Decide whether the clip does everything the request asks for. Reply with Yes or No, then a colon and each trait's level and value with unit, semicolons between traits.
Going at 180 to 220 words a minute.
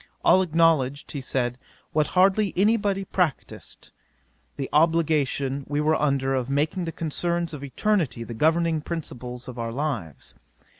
No: average, 145 wpm